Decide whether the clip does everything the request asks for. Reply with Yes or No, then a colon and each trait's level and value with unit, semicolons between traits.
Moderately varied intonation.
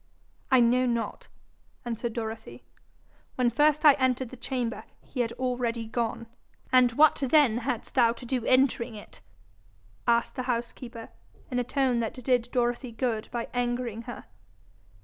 No: narrow, 1.6 semitones